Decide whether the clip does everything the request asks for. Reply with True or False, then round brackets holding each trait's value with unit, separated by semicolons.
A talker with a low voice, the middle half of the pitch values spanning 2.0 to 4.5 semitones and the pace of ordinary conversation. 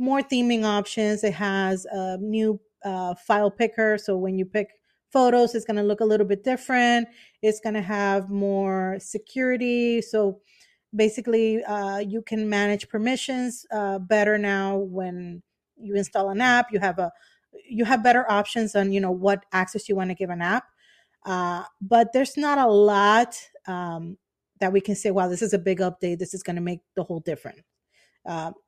False (205 Hz; 2.9 semitones; 185 wpm)